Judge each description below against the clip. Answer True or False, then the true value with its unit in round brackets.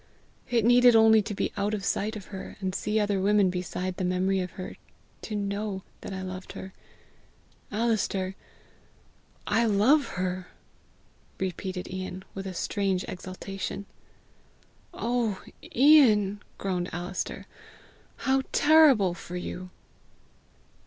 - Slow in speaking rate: True (125 wpm)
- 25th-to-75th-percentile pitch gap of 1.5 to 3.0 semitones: True (2.7 semitones)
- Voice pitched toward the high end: True (195 Hz)